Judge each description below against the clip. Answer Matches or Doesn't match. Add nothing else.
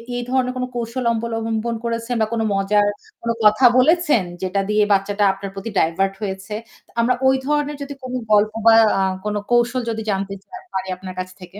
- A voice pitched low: Doesn't match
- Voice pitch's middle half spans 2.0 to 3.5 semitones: Doesn't match